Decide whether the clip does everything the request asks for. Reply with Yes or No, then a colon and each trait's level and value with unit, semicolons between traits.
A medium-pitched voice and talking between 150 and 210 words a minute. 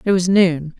No: medium, 180 Hz; fast, 225 wpm